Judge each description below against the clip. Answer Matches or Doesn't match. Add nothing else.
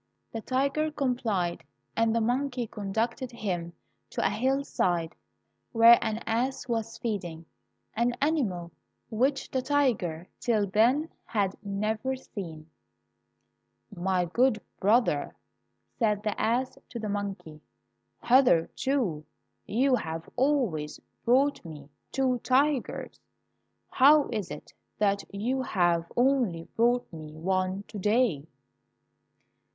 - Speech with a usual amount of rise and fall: Doesn't match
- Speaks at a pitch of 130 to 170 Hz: Doesn't match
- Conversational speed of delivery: Doesn't match